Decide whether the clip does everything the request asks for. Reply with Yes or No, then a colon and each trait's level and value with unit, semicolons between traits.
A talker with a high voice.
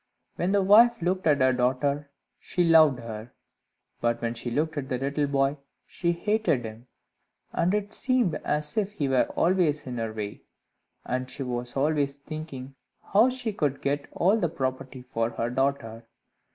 No: medium, 140 Hz